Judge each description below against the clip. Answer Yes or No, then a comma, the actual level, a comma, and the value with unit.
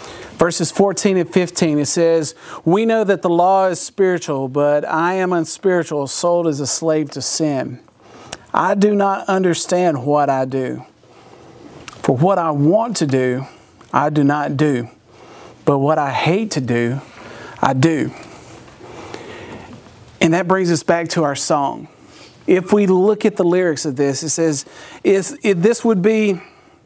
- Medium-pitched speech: Yes, medium, 165 Hz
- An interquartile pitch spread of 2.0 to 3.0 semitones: No, average, 4.7 semitones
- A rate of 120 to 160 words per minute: Yes, average, 155 wpm